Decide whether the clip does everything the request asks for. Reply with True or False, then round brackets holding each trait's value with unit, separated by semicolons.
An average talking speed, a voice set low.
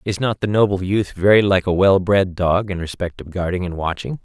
False (240 wpm; 95 Hz)